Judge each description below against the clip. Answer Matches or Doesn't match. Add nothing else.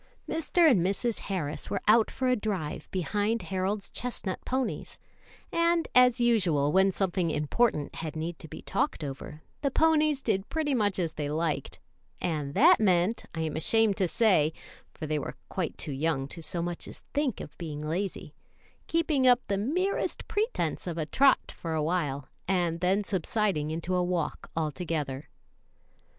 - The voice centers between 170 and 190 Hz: Matches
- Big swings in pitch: Matches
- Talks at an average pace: Matches